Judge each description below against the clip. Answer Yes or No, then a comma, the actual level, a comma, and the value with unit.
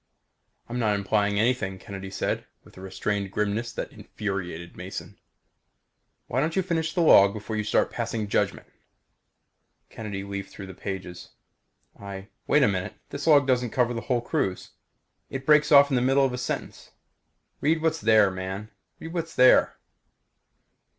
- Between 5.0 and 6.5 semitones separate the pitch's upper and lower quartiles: Yes, wide, 5.4 semitones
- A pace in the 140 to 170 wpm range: Yes, average, 160 wpm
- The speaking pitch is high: No, low, 110 Hz